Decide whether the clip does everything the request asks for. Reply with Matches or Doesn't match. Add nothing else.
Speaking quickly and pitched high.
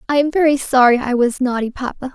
Matches